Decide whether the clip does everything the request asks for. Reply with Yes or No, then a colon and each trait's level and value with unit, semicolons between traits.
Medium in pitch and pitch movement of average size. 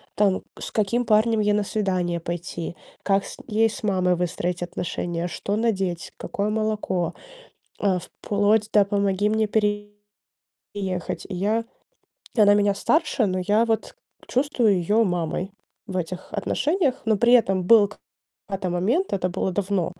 No: high, 205 Hz; average, 3.0 semitones